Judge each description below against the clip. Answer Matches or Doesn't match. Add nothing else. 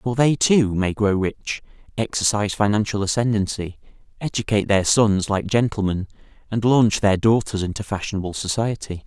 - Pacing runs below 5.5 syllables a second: Matches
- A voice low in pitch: Matches